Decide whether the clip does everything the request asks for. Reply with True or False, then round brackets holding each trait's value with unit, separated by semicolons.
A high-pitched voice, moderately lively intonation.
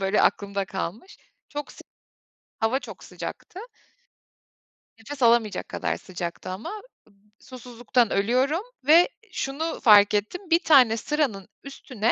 False (240 Hz; 5.9 semitones)